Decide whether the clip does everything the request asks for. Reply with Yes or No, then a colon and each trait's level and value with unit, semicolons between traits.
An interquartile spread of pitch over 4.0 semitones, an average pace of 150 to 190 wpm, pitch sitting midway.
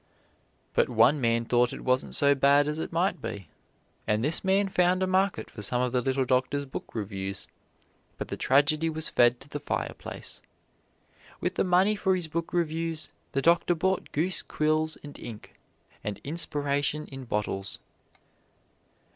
Yes: average, 5.1 semitones; average, 165 wpm; medium, 145 Hz